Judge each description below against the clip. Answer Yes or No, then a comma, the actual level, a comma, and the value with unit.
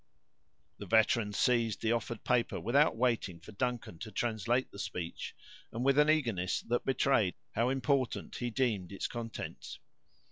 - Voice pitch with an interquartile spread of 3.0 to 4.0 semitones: Yes, average, 3.3 semitones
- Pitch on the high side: No, low, 115 Hz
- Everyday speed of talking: Yes, average, 150 wpm